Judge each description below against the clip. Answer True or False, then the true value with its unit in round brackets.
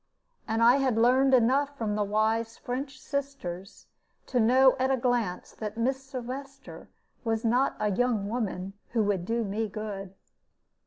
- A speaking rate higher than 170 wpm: False (155 wpm)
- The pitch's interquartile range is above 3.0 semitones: True (3.6 semitones)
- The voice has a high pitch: True (230 Hz)